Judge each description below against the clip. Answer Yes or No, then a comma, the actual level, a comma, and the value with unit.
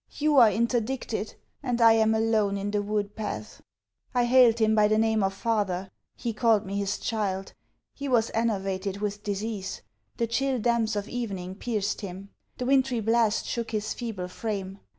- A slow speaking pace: No, average, 170 wpm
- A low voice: No, high, 220 Hz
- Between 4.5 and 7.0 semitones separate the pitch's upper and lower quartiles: No, narrow, 2.6 semitones